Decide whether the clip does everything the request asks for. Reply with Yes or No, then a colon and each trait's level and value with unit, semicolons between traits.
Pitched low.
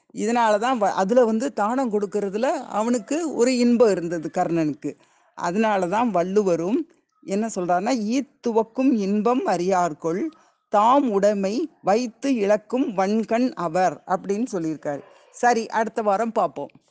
No: high, 220 Hz